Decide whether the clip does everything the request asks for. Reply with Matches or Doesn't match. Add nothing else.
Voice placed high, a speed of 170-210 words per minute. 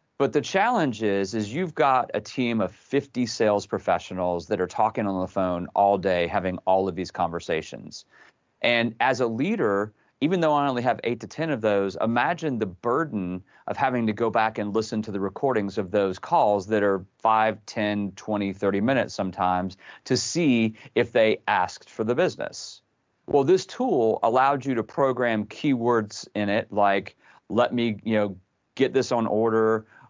Doesn't match